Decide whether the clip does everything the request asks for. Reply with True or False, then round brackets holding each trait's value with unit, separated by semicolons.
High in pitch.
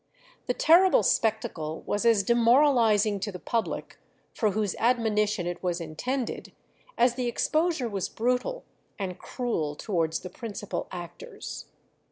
True (220 Hz)